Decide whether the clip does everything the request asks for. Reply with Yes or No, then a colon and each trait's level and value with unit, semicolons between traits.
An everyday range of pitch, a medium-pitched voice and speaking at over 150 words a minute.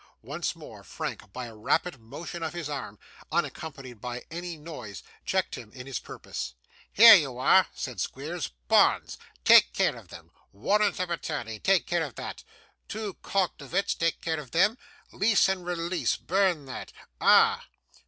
No: wide, 6.1 semitones; medium, 160 Hz; average, 160 wpm